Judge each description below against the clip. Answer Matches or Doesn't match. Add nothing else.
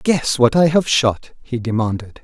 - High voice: Doesn't match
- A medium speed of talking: Matches